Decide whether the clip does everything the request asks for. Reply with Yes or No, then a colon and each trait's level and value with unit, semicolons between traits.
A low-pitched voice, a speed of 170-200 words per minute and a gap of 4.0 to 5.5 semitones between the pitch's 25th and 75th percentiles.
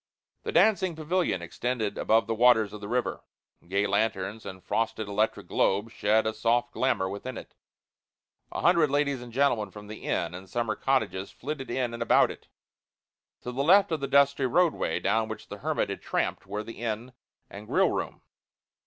Yes: low, 115 Hz; average, 180 wpm; average, 4.4 semitones